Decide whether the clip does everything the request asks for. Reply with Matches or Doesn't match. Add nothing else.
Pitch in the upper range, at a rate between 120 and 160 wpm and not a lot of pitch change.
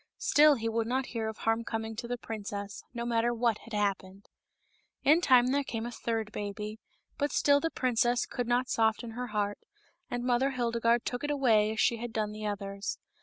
Doesn't match